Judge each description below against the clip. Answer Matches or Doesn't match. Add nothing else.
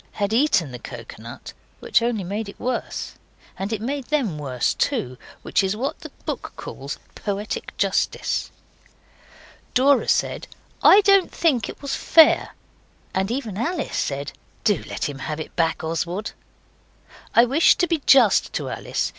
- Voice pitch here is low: Doesn't match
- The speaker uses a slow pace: Doesn't match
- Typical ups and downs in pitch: Doesn't match